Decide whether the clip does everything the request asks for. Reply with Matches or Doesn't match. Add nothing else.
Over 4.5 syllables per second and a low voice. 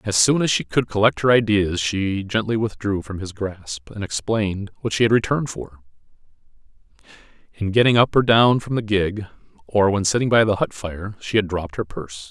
Matches